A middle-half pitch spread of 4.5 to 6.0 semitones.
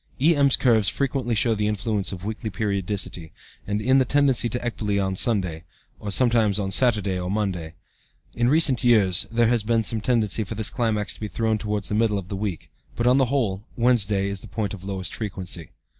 No: average, 3.2 semitones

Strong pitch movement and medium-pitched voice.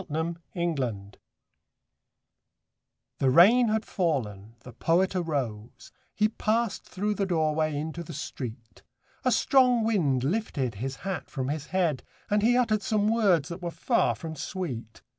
Yes: wide, 7.7 semitones; medium, 165 Hz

